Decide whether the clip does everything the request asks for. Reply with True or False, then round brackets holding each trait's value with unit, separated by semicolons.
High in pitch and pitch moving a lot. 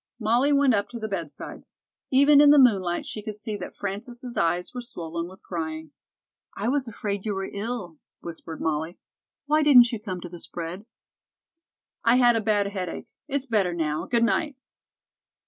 True (210 Hz; 5.9 semitones)